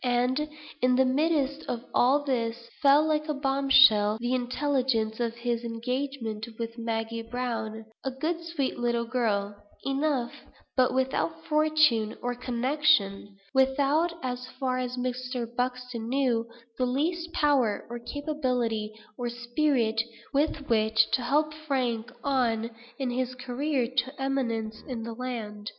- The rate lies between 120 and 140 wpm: Yes, slow, 135 wpm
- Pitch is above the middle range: Yes, very high, 250 Hz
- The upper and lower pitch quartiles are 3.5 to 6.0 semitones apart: No, average, 3.1 semitones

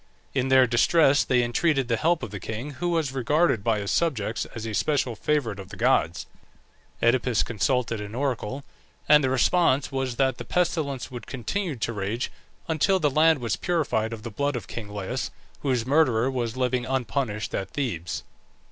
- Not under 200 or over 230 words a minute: No, average, 180 wpm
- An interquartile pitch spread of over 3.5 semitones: Yes, average, 4.2 semitones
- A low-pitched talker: Yes, low, 125 Hz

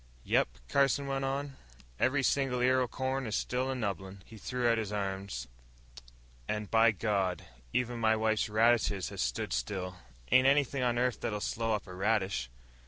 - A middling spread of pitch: Yes, average, 4.2 semitones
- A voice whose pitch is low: Yes, low, 115 Hz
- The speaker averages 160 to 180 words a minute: Yes, average, 170 wpm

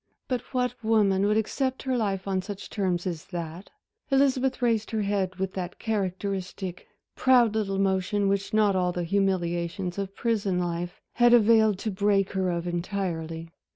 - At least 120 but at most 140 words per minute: No, average, 160 wpm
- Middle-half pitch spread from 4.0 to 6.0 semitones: No, average, 3.2 semitones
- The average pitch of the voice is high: Yes, high, 195 Hz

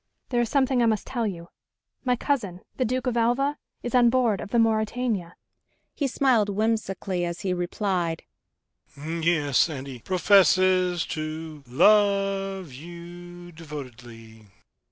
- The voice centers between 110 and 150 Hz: No, high, 190 Hz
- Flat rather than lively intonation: No, wide, 5.5 semitones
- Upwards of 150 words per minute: No, slow, 135 wpm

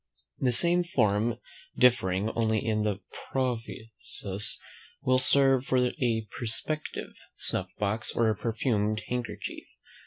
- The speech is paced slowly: Yes, slow, 105 wpm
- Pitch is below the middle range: Yes, low, 115 Hz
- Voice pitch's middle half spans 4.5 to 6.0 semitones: No, average, 3.2 semitones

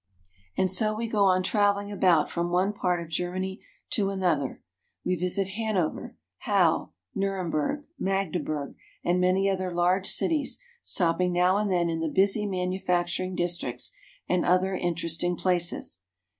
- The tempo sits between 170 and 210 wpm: No, average, 145 wpm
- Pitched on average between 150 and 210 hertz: Yes, medium, 185 Hz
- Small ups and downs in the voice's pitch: Yes, narrow, 1.9 semitones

